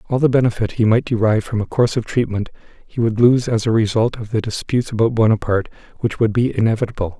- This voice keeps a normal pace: No, fast, 215 wpm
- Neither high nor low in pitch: No, low, 115 Hz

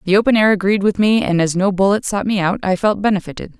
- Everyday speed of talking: No, fast, 265 wpm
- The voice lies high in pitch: Yes, high, 200 Hz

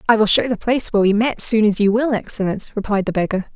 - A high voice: Yes, high, 215 Hz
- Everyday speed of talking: No, fast, 270 wpm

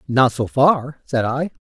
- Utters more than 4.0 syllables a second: No, 3.7 syllables/s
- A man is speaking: Yes, male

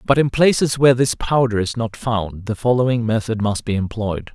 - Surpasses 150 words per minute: Yes, fast, 205 wpm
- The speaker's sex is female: No, male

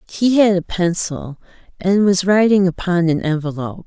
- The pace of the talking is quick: No, average, 155 wpm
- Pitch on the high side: No, medium, 180 Hz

